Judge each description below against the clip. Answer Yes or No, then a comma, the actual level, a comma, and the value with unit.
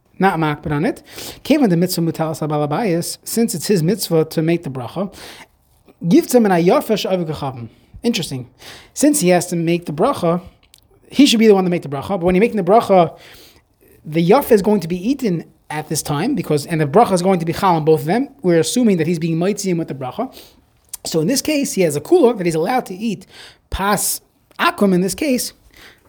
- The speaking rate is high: Yes, fast, 215 wpm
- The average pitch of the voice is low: No, medium, 180 Hz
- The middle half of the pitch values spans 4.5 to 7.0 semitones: Yes, average, 5.1 semitones